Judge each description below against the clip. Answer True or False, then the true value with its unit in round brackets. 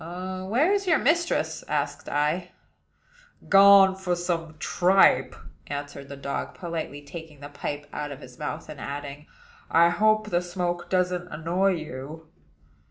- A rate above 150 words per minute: False (140 wpm)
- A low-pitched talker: False (170 Hz)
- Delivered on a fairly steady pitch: False (4.3 semitones)